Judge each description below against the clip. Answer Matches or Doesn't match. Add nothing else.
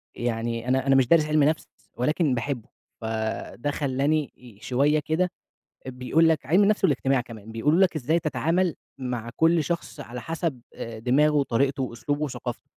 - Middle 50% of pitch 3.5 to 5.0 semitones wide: Matches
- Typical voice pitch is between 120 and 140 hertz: Matches